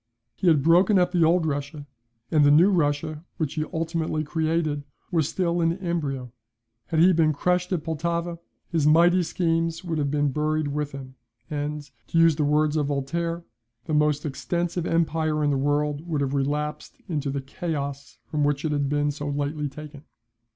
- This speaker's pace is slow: No, average, 180 wpm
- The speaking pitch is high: No, medium, 155 Hz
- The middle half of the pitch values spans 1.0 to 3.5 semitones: Yes, narrow, 2.4 semitones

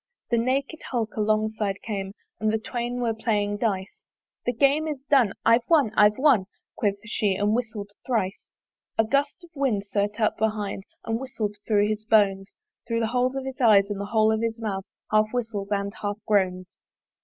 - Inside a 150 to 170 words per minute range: No, average, 185 wpm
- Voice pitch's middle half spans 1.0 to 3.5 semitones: Yes, average, 3.0 semitones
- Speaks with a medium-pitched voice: No, high, 220 Hz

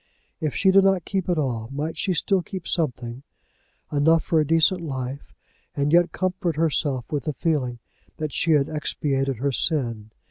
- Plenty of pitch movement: No, average, 3.8 semitones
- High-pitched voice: No, medium, 155 Hz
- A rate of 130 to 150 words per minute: No, average, 170 wpm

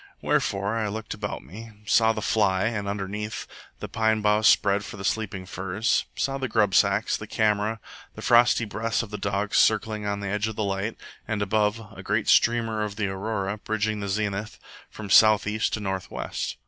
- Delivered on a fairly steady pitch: Yes, narrow, 1.7 semitones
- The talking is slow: No, average, 195 wpm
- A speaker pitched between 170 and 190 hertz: No, low, 105 Hz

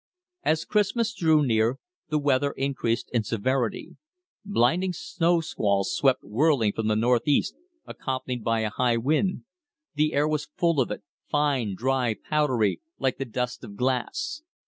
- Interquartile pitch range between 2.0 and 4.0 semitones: No, average, 4.8 semitones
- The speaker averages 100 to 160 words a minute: Yes, average, 145 wpm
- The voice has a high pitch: No, low, 130 Hz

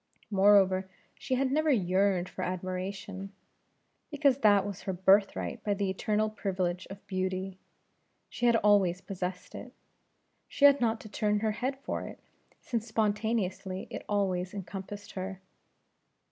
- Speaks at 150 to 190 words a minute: No, average, 140 wpm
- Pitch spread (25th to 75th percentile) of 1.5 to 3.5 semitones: Yes, narrow, 2.5 semitones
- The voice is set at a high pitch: Yes, high, 200 Hz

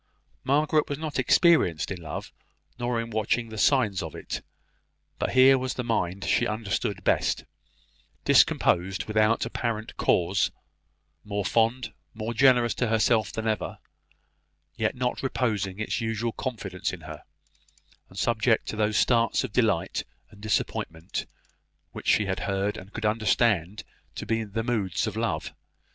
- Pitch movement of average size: Yes, average, 3.2 semitones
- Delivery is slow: No, average, 145 wpm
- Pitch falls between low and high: No, low, 110 Hz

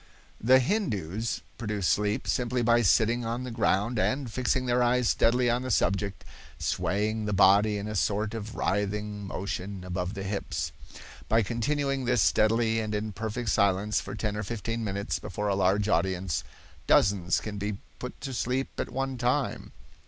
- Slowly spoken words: No, average, 165 wpm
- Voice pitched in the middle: No, low, 110 Hz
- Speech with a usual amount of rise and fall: Yes, average, 3.2 semitones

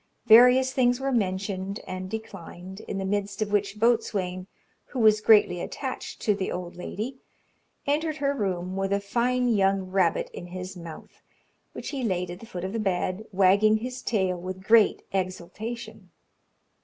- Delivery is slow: No, average, 165 wpm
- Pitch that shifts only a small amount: No, average, 3.7 semitones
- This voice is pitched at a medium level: No, high, 200 Hz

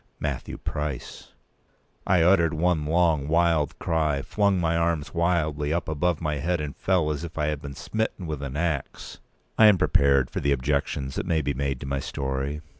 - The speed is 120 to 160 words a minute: No, average, 190 wpm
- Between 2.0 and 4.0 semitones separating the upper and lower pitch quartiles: Yes, average, 3.2 semitones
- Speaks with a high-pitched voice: No, very low, 75 Hz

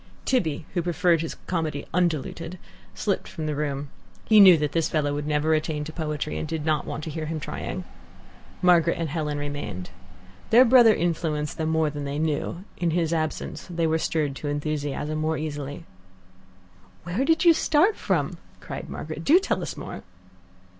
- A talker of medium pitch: Yes, medium, 160 Hz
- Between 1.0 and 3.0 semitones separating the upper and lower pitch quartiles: Yes, narrow, 2.6 semitones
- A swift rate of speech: No, average, 175 wpm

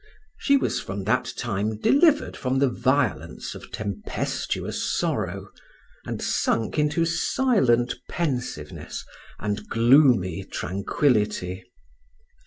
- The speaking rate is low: Yes, slow, 95 wpm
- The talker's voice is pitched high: No, low, 120 Hz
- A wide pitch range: Yes, wide, 6.4 semitones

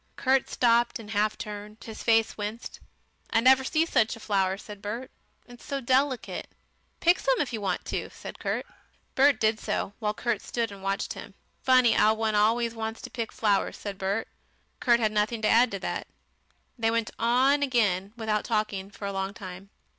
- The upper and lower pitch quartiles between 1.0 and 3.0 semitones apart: Yes, narrow, 2.6 semitones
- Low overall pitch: No, high, 225 Hz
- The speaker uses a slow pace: No, average, 190 wpm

